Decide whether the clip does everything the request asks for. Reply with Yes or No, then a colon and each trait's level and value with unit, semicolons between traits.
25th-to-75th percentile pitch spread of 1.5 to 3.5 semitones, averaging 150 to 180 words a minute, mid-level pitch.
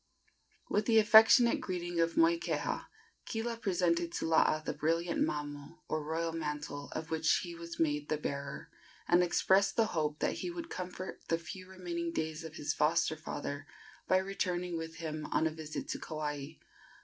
Yes: average, 3.1 semitones; average, 170 wpm; medium, 165 Hz